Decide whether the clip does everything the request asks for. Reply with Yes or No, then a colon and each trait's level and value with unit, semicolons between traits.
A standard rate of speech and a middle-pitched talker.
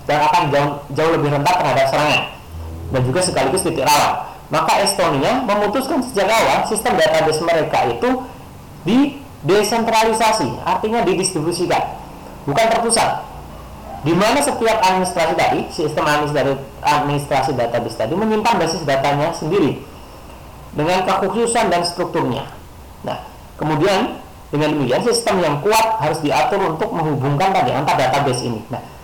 Yes: average, 130 wpm; medium, 170 Hz